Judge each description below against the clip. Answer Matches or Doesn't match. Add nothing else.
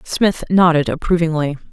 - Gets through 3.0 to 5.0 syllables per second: Doesn't match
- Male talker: Doesn't match